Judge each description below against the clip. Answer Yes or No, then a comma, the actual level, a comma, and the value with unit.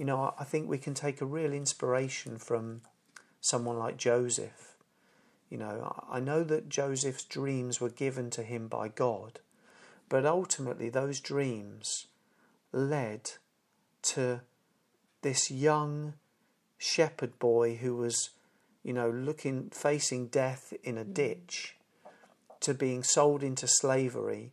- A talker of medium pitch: No, low, 130 Hz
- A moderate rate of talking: No, slow, 125 wpm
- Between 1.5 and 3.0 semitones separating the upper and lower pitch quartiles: Yes, narrow, 2.6 semitones